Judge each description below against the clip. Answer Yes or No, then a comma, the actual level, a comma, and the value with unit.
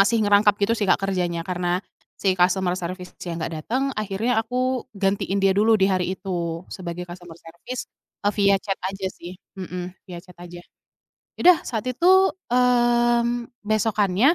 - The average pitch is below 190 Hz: No, high, 195 Hz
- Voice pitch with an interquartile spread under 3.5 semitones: No, average, 4.6 semitones